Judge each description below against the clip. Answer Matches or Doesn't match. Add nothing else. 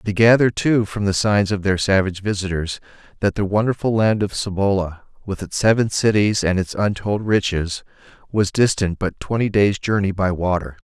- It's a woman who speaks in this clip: Doesn't match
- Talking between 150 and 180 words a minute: Matches